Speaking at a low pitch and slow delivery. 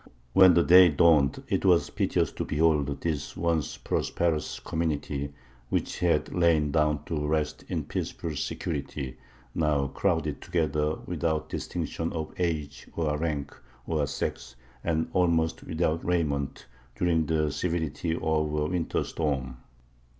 Yes: very low, 80 Hz; slow, 130 wpm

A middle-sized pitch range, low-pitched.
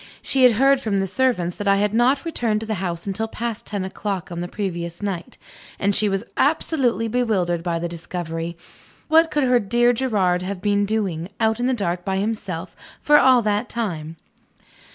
No: average, 5.0 semitones; high, 205 Hz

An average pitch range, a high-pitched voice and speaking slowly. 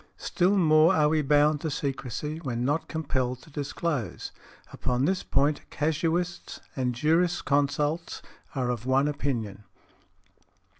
No: average, 3.4 semitones; medium, 145 Hz; slow, 120 wpm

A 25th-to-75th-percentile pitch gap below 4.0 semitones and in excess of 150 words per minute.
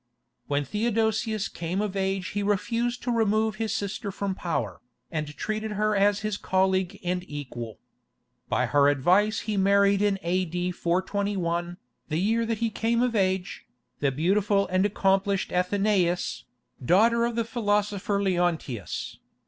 No: average, 3.1 semitones; average, 140 wpm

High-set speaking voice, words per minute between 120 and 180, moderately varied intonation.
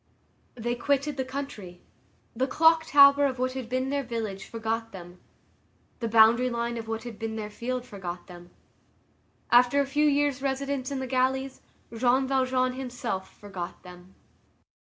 Yes: very high, 250 Hz; average, 155 wpm; average, 3.2 semitones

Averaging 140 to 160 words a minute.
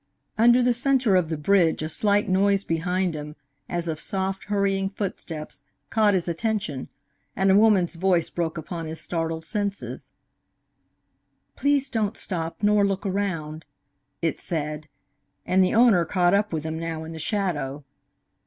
Yes: average, 155 wpm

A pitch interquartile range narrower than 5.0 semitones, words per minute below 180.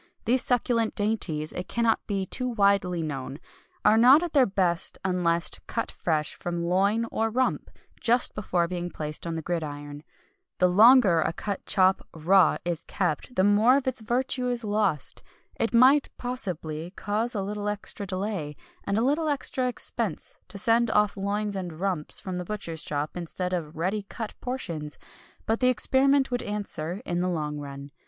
No: average, 5.3 semitones; average, 170 wpm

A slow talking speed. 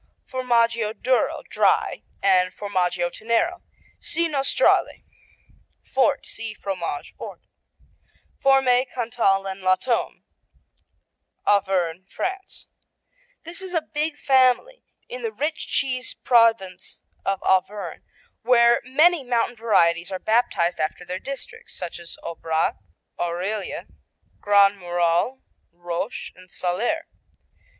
Yes: slow, 105 wpm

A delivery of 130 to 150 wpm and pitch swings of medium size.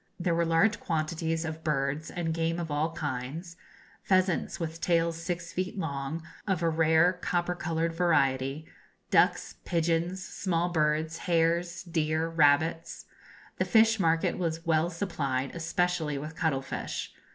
No: average, 140 wpm; narrow, 1.7 semitones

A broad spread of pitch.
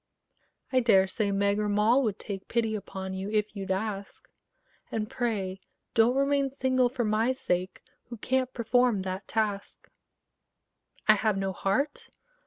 No: average, 3.8 semitones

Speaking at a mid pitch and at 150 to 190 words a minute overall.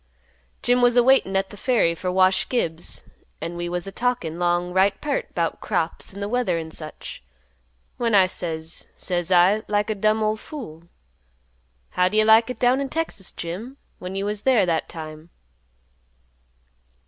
No: high, 195 Hz; average, 170 wpm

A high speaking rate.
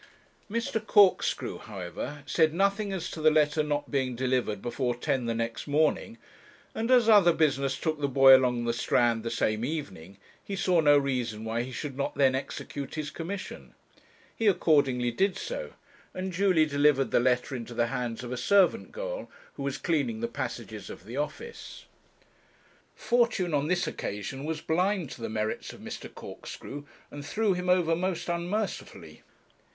No: average, 170 wpm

